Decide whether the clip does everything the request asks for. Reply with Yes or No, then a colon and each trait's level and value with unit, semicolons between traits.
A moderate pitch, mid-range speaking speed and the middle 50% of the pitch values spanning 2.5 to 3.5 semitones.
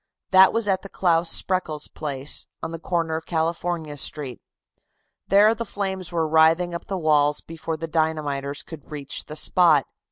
Yes: medium, 165 Hz; average, 165 wpm; average, 3.0 semitones